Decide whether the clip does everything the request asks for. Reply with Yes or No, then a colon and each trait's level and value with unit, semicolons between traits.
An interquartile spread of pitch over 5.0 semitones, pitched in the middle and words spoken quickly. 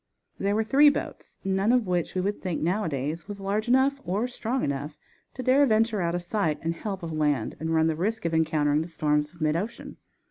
Yes: wide, 5.4 semitones; medium, 180 Hz; fast, 220 wpm